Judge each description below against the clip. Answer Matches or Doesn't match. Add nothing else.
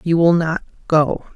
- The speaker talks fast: Doesn't match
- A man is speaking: Doesn't match